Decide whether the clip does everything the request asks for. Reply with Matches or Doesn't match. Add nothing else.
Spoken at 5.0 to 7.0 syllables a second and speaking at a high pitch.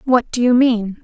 Doesn't match